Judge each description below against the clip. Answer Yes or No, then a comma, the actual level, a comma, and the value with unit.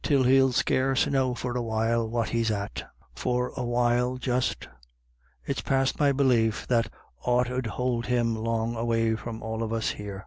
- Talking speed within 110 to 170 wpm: No, average, 180 wpm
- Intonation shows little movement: Yes, narrow, 2.0 semitones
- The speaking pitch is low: Yes, low, 120 Hz